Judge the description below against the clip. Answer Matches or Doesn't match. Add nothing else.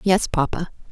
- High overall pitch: Doesn't match